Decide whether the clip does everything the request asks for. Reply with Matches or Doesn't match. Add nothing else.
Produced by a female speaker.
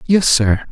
Doesn't match